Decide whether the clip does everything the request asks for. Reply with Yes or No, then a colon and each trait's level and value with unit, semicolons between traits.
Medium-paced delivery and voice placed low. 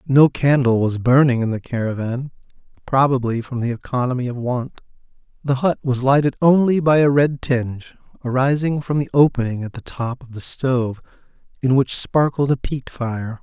Yes: average, 170 wpm; low, 130 Hz